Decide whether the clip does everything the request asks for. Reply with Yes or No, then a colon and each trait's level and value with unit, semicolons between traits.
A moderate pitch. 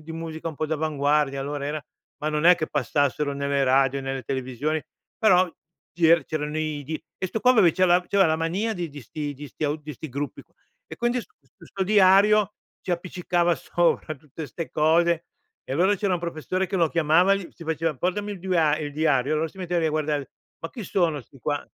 Yes: medium, 160 Hz